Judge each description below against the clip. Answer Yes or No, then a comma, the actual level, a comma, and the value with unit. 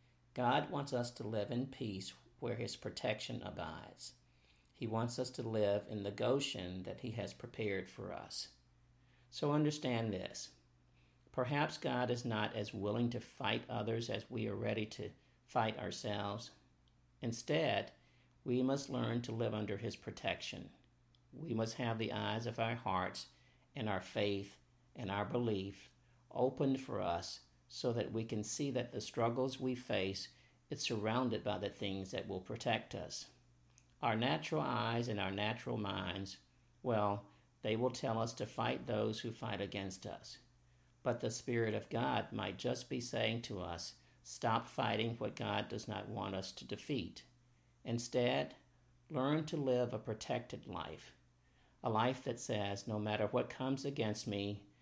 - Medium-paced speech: Yes, average, 160 wpm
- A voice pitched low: Yes, low, 110 Hz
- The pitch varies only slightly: No, average, 3.6 semitones